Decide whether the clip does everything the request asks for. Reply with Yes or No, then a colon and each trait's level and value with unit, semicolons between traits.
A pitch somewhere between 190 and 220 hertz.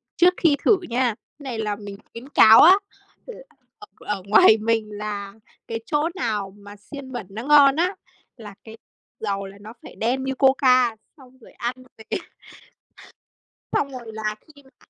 No: high, 235 Hz